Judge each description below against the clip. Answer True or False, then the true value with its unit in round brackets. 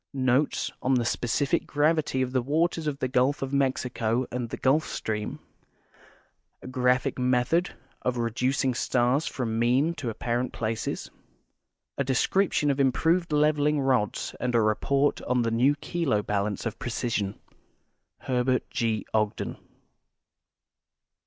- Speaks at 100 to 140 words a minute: True (135 wpm)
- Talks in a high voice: False (130 Hz)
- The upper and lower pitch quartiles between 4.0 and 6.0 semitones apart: False (3.4 semitones)